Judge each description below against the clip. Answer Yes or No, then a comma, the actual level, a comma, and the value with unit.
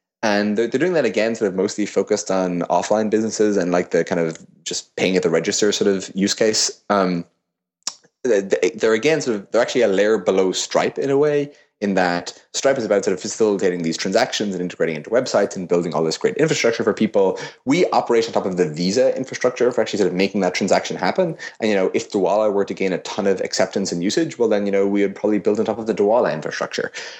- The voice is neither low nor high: No, low, 100 Hz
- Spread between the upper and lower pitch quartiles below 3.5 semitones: Yes, average, 3.1 semitones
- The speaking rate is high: Yes, fast, 235 wpm